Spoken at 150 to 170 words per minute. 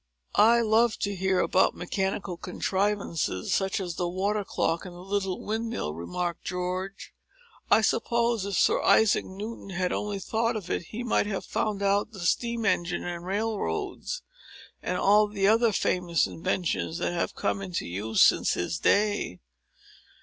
Yes: average, 155 wpm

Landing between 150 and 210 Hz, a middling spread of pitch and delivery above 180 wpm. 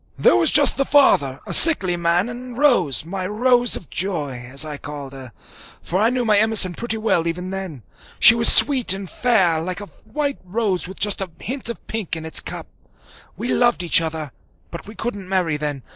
No: high, 190 Hz; wide, 6.2 semitones; fast, 205 wpm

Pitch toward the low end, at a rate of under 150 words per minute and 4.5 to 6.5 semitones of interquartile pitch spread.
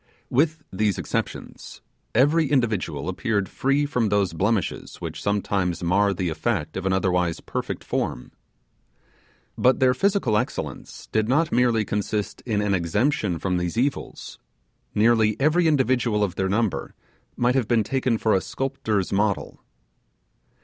Yes: low, 105 Hz; average, 140 wpm; average, 5.1 semitones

